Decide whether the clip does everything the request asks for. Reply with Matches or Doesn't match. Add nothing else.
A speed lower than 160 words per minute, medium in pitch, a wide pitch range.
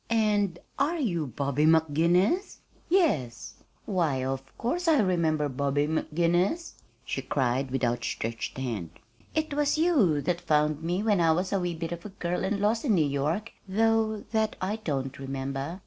Doesn't match